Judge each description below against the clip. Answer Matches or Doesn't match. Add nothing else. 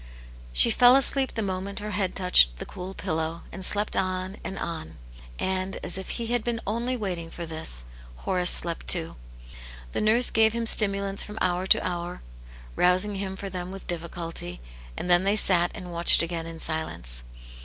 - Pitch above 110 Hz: Matches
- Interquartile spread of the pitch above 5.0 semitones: Doesn't match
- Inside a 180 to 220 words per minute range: Matches